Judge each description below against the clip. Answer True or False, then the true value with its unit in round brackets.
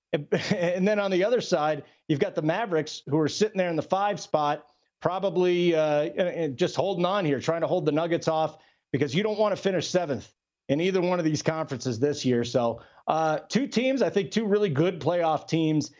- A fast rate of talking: True (210 wpm)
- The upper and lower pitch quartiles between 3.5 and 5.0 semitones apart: True (3.9 semitones)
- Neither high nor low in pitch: True (165 Hz)